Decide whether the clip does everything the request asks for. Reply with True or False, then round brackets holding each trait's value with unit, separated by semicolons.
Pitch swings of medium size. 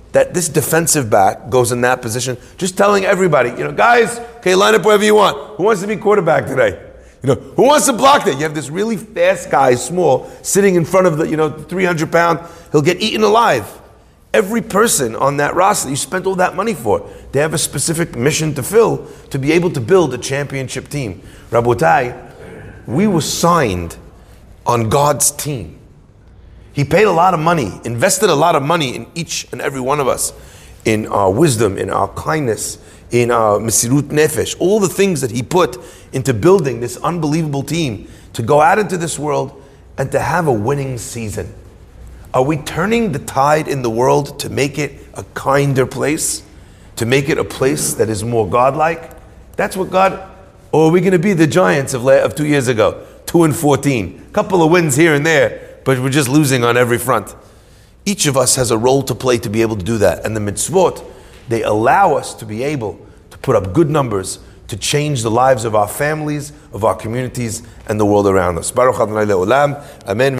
False (6.6 semitones)